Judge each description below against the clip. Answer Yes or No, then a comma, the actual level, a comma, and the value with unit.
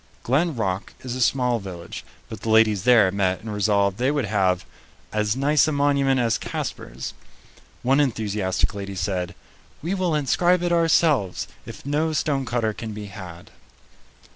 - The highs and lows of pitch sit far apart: Yes, wide, 6.2 semitones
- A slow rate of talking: No, average, 155 wpm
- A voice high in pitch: No, low, 115 Hz